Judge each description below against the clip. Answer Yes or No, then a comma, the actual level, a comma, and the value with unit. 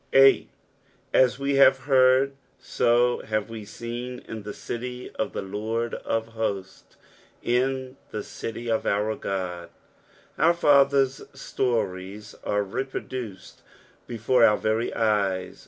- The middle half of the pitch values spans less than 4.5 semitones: Yes, average, 3.6 semitones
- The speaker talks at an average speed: No, slow, 125 wpm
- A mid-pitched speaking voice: No, low, 115 Hz